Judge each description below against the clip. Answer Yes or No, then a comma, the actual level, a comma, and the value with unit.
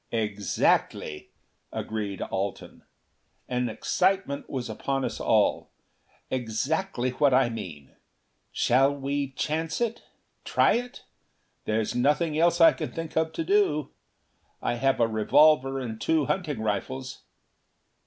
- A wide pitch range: Yes, wide, 6.0 semitones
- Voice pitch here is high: No, low, 135 Hz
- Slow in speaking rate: Yes, slow, 120 wpm